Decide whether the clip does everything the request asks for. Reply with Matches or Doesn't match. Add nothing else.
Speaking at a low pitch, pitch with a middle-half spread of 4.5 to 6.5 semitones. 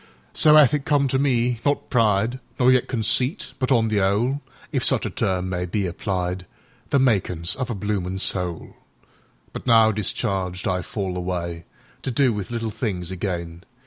Matches